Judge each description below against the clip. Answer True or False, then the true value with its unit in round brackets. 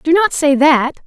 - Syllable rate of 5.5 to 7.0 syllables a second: False (3.9 syllables/s)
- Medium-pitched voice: False (300 Hz)